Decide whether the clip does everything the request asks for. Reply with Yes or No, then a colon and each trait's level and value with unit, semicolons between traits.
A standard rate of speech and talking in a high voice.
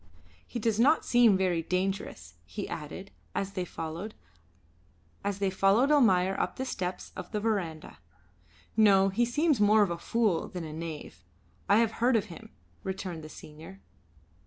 Yes: average, 150 wpm; high, 195 Hz